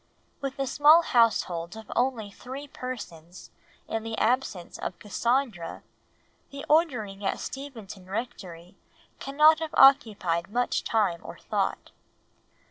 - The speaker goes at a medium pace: No, slow, 120 wpm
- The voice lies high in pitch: Yes, high, 230 Hz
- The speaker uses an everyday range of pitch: No, wide, 5.7 semitones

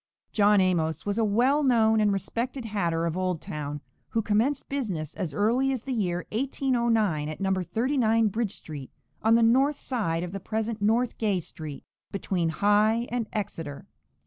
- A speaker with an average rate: Yes, average, 170 wpm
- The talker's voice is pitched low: No, high, 210 Hz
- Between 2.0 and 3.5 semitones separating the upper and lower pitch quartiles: No, average, 4.7 semitones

